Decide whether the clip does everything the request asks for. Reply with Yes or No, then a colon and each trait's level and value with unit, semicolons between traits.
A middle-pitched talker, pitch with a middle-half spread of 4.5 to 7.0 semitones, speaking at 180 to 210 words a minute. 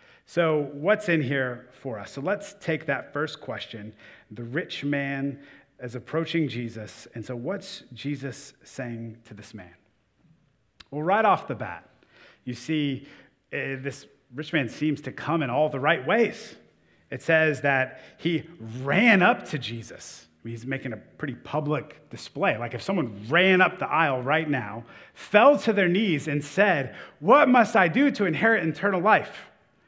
No: medium, 145 Hz; wide, 5.4 semitones; average, 165 wpm